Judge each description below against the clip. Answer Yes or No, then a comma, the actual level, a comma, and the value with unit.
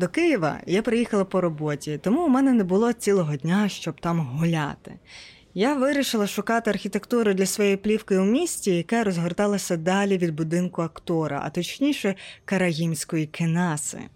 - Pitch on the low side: No, high, 190 Hz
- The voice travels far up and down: No, average, 4.2 semitones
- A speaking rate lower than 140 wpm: No, average, 150 wpm